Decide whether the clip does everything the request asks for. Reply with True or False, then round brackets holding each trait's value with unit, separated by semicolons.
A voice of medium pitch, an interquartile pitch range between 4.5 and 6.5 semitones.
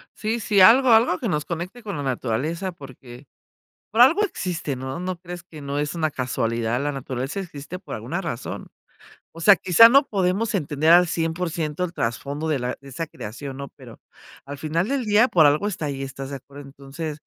True (160 Hz; 5.1 semitones)